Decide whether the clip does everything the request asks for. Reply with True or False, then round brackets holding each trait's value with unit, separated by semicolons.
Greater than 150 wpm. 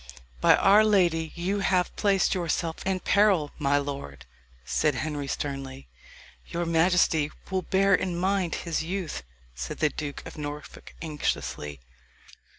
False (135 wpm)